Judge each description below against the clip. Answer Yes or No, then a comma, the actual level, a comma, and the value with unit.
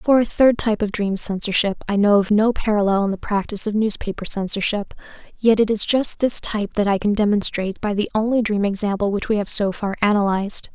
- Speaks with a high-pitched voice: Yes, high, 210 Hz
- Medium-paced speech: No, fast, 220 wpm